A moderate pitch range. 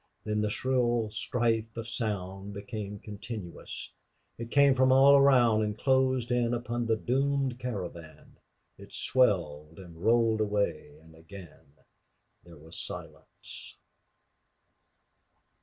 Yes: average, 4.3 semitones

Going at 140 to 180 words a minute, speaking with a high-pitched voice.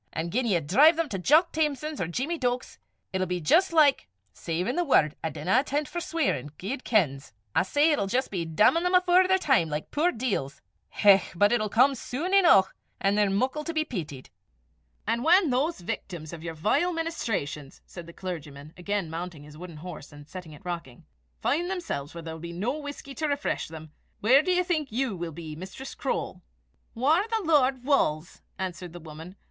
No: average, 200 wpm; high, 210 Hz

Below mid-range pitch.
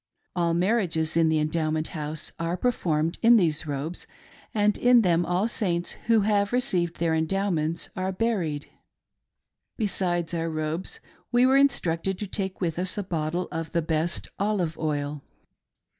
No: medium, 175 Hz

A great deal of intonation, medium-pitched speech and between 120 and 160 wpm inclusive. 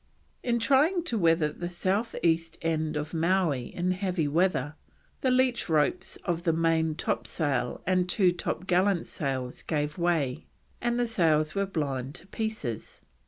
No: average, 4.0 semitones; medium, 170 Hz; average, 150 wpm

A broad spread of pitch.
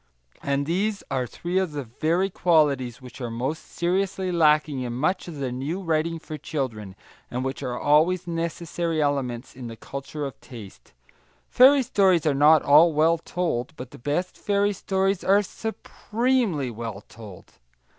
Yes: wide, 5.8 semitones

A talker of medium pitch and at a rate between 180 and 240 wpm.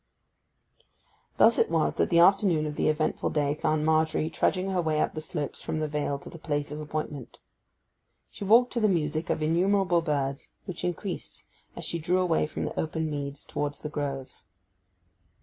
Yes: medium, 155 Hz; average, 185 wpm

